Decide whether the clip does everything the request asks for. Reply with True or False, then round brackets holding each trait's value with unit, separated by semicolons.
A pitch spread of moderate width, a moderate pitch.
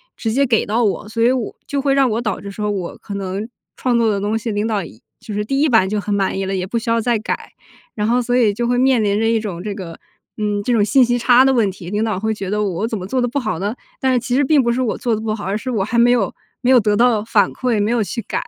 False (3.0 semitones; 220 Hz)